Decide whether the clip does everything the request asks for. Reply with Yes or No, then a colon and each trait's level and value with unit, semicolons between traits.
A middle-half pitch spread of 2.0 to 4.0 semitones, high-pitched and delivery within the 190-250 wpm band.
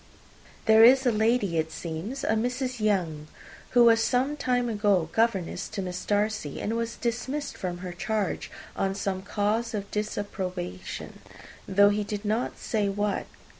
No: average, 3.4 semitones; high, 210 Hz; average, 155 wpm